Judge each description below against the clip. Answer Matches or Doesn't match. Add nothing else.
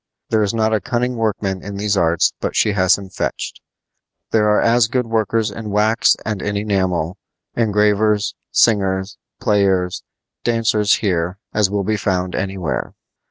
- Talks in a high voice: Doesn't match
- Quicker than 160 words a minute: Doesn't match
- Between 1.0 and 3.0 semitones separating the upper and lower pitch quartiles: Matches